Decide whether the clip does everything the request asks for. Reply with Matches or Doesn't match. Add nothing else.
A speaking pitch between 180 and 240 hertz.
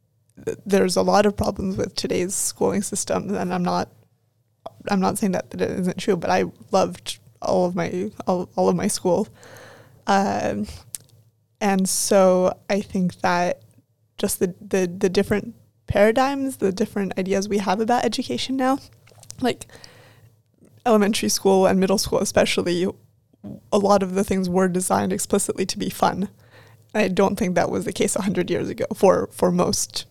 Matches